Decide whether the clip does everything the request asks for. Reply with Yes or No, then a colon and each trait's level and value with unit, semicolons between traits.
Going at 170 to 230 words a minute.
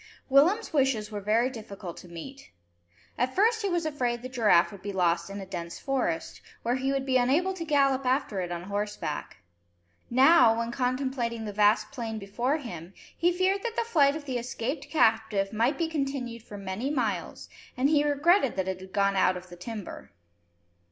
Yes: average, 190 wpm